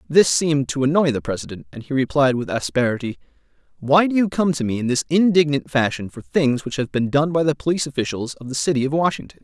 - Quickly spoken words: Yes, fast, 230 wpm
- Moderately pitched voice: Yes, medium, 145 Hz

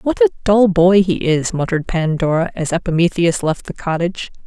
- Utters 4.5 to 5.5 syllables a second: Yes, 5.4 syllables/s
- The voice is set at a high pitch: No, medium, 170 Hz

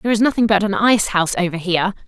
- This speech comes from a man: No, female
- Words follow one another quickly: Yes, fast, 260 wpm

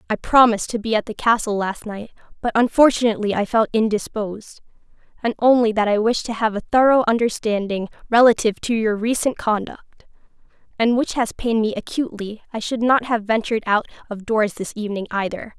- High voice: Yes, high, 220 Hz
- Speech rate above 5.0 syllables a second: Yes, 5.9 syllables/s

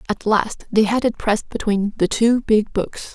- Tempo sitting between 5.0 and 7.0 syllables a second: No, 4.5 syllables/s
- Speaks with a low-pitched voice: No, high, 215 Hz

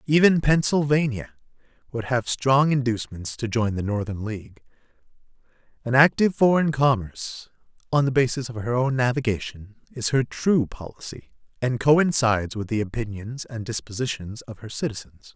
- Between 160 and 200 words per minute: No, average, 140 wpm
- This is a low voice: Yes, low, 120 Hz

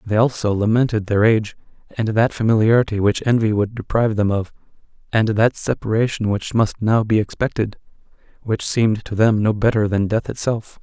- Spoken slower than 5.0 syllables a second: No, 5.5 syllables/s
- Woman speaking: No, male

